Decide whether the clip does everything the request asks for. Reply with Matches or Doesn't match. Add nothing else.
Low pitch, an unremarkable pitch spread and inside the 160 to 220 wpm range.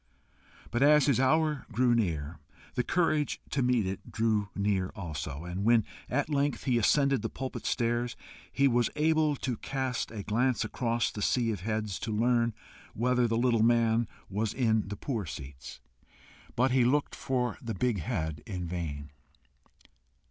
Matches